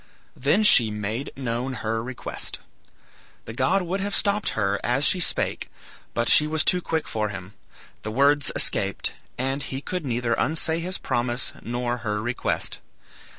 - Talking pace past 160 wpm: No, average, 155 wpm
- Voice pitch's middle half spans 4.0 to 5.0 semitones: No, wide, 5.6 semitones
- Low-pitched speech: Yes, low, 125 Hz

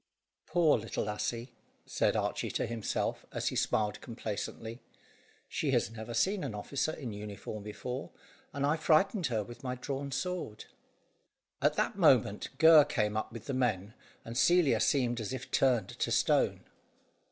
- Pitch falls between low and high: No, low, 120 Hz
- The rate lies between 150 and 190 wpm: Yes, average, 155 wpm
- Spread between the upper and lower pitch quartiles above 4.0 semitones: Yes, average, 4.7 semitones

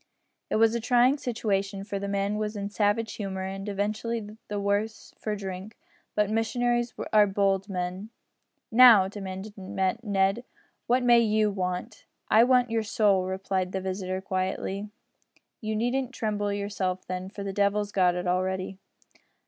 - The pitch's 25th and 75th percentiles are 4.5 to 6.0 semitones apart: No, narrow, 2.4 semitones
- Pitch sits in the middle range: No, high, 205 Hz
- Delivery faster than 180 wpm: No, average, 155 wpm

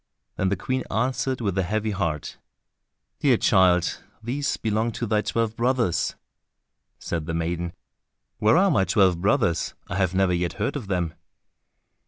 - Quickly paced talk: No, average, 155 wpm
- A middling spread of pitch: Yes, average, 4.7 semitones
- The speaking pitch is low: Yes, low, 100 Hz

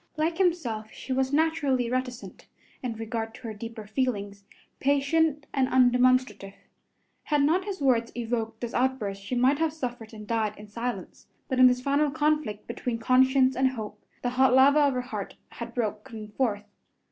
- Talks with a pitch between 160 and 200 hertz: No, very high, 250 Hz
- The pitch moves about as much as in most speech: Yes, average, 3.4 semitones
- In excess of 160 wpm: Yes, average, 170 wpm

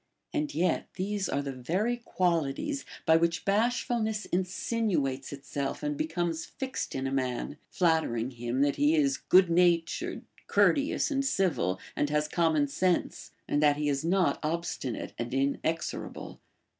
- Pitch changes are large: Yes, wide, 5.8 semitones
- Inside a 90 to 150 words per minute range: Yes, average, 145 wpm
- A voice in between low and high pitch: Yes, medium, 165 Hz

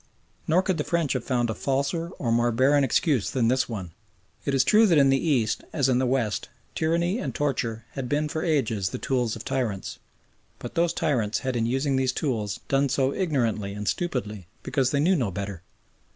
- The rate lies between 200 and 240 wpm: Yes, fast, 205 wpm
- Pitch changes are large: No, average, 4.4 semitones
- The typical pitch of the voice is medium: No, low, 130 Hz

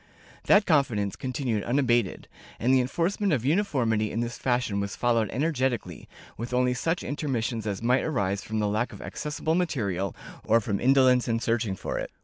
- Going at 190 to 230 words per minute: No, average, 170 wpm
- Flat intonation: No, average, 3.9 semitones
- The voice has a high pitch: No, low, 120 Hz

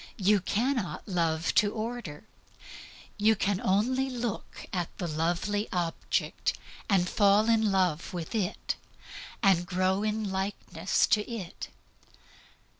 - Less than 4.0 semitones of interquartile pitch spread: Yes, average, 3.4 semitones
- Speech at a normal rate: No, slow, 115 wpm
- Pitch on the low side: No, high, 200 Hz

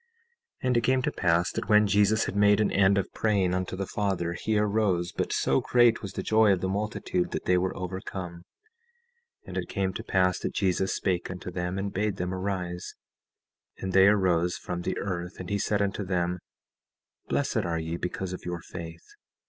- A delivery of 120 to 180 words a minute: No, fast, 205 wpm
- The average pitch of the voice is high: No, very low, 95 Hz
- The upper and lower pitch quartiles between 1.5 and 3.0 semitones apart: Yes, narrow, 2.4 semitones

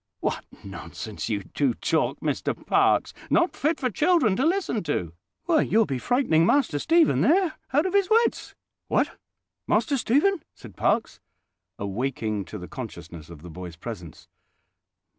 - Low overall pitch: No, high, 215 Hz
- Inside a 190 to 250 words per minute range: No, average, 145 wpm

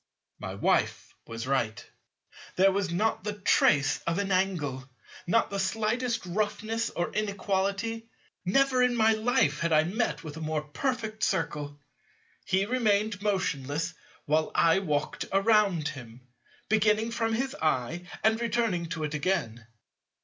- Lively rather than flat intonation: Yes, wide, 6.1 semitones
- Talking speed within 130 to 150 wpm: Yes, average, 140 wpm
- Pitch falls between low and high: No, high, 195 Hz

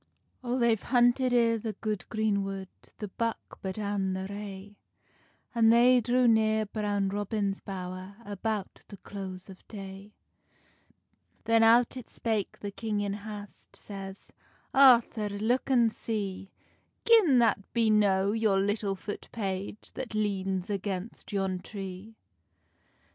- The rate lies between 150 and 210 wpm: No, slow, 135 wpm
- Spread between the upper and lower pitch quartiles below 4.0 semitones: Yes, narrow, 2.6 semitones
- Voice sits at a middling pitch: No, high, 205 Hz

